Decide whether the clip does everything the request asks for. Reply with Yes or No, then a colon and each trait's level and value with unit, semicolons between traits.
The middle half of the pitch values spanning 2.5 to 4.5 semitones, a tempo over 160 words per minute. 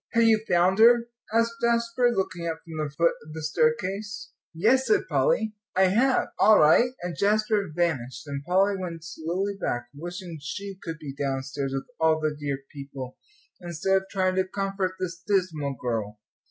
No: average, 4.9 semitones; average, 170 wpm